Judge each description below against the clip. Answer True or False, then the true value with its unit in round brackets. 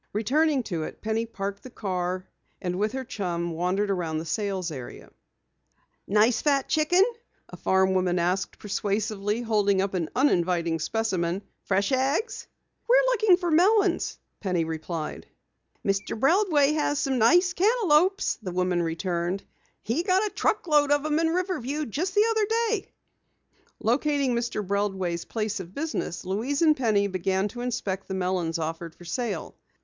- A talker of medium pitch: False (215 Hz)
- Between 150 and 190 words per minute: True (155 wpm)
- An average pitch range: False (8.4 semitones)